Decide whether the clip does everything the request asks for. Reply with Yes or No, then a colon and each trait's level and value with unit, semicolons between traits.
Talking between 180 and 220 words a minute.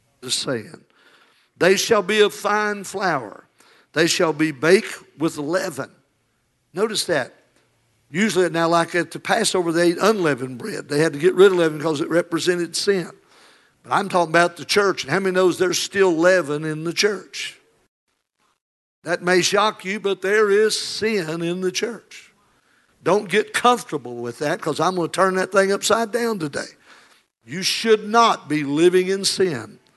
No: average, 170 wpm